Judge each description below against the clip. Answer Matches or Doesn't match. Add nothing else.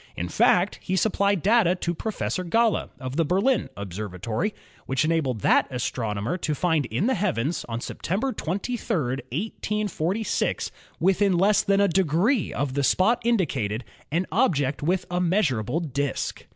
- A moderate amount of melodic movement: Doesn't match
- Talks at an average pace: Matches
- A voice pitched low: Doesn't match